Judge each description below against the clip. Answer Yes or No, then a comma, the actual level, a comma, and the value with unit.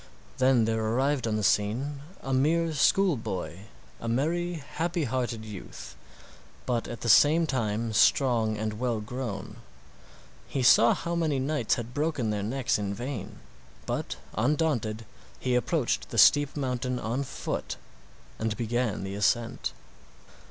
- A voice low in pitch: Yes, low, 120 Hz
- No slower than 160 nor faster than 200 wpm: No, average, 140 wpm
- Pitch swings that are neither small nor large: Yes, average, 4.4 semitones